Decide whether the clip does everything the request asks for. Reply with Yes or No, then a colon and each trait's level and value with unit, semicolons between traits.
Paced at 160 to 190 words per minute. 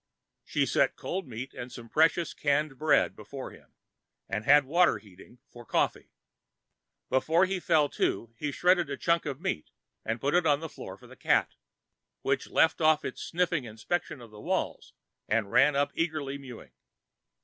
Yes: average, 170 wpm